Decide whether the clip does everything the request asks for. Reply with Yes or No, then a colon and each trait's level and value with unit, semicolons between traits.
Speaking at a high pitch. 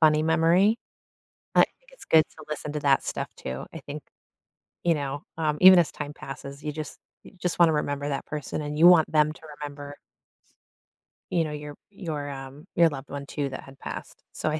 No: medium, 150 Hz